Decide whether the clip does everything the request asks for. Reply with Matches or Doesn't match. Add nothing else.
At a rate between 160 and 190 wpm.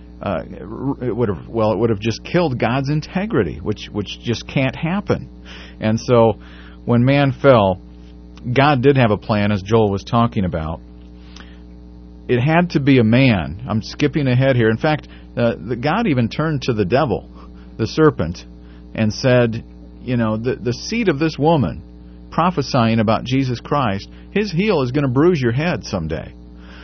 Matches